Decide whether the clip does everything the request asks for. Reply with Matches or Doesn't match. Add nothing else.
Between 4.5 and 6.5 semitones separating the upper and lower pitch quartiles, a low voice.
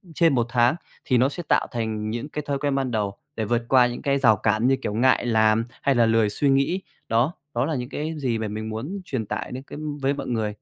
Doesn't match